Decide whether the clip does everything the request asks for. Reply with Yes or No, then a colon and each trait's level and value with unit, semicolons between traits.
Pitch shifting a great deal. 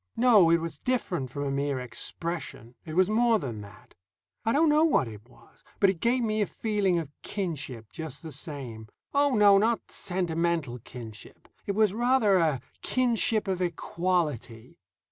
Yes: wide, 7.8 semitones